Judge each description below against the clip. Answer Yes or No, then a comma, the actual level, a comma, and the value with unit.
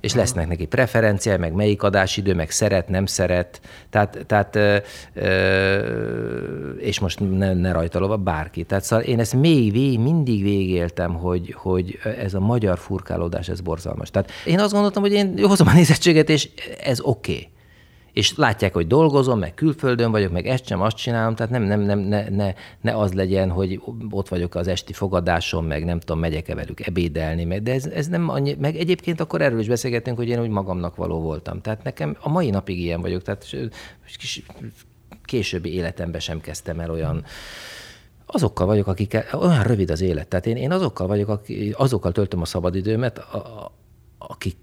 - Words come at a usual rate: No, fast, 180 wpm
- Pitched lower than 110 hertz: Yes, low, 100 Hz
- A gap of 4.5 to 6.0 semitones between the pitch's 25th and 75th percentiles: Yes, average, 4.9 semitones